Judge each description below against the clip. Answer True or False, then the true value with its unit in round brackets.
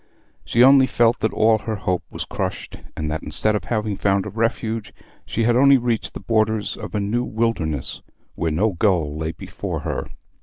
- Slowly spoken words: False (190 wpm)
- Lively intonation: False (3.3 semitones)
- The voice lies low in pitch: True (110 Hz)